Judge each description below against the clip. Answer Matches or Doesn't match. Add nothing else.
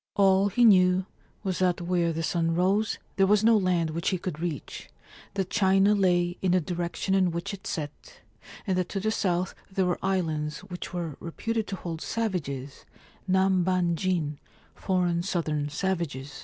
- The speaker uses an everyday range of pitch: Doesn't match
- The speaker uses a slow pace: Doesn't match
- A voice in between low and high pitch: Matches